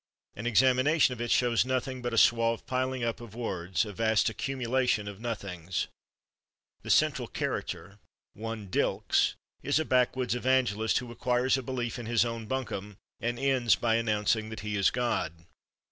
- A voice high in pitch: No, low, 115 Hz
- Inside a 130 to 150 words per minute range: No, average, 160 wpm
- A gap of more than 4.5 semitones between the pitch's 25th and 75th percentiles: No, average, 3.0 semitones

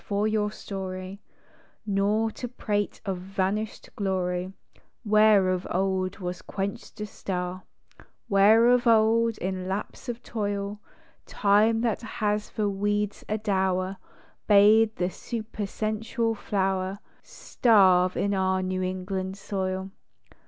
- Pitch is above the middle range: Yes, high, 200 Hz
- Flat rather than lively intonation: Yes, narrow, 2.3 semitones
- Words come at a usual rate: No, slow, 115 wpm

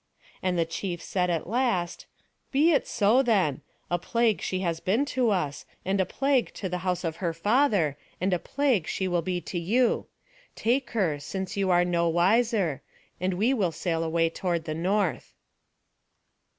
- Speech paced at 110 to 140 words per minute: No, average, 175 wpm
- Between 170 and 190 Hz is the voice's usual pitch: Yes, medium, 185 Hz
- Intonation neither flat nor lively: Yes, average, 4.7 semitones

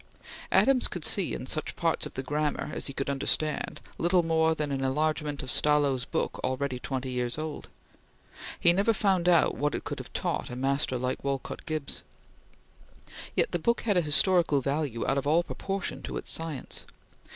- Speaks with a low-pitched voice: No, medium, 150 Hz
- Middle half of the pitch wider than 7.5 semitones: No, average, 3.7 semitones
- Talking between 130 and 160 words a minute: No, average, 185 wpm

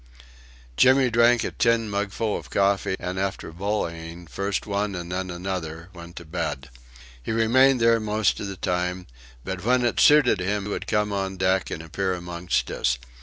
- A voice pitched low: Yes, very low, 95 Hz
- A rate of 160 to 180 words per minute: Yes, average, 170 wpm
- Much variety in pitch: No, average, 3.5 semitones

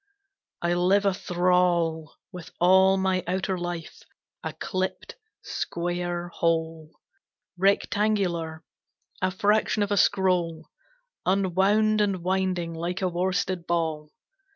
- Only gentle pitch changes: Yes, narrow, 1.9 semitones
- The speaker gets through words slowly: Yes, slow, 105 wpm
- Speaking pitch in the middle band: Yes, medium, 180 Hz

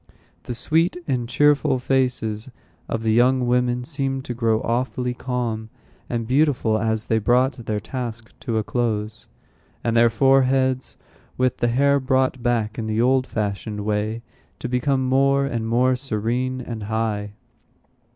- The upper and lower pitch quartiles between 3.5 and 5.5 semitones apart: No, average, 2.8 semitones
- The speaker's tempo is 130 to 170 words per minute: Yes, average, 150 wpm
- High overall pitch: No, low, 120 Hz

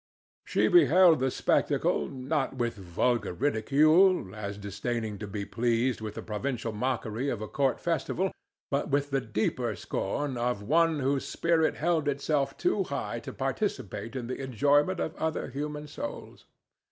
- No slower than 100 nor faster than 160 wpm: Yes, average, 155 wpm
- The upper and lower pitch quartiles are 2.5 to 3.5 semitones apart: No, average, 4.8 semitones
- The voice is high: No, low, 130 Hz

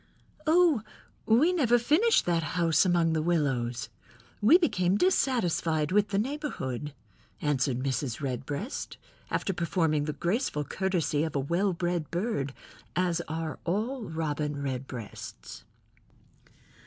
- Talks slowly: Yes, slow, 115 wpm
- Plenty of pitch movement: Yes, wide, 6.2 semitones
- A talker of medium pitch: Yes, medium, 170 Hz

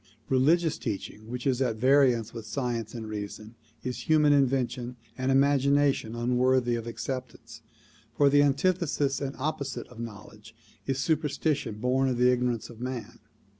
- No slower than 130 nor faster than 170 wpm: Yes, average, 155 wpm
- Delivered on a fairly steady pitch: No, average, 3.1 semitones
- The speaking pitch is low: Yes, low, 125 Hz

